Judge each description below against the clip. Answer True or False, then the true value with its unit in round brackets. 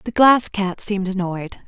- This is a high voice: True (200 Hz)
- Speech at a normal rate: True (180 wpm)